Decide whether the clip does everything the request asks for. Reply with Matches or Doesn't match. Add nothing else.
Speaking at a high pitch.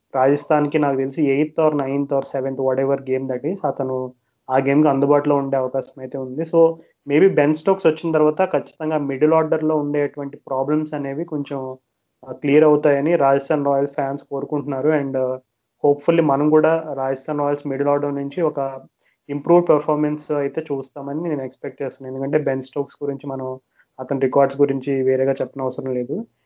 Doesn't match